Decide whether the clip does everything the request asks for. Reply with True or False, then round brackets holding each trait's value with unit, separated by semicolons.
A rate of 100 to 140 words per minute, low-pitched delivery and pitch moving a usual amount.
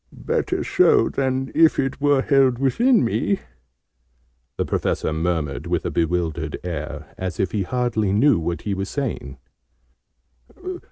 False (135 wpm; 110 Hz; 7.7 semitones)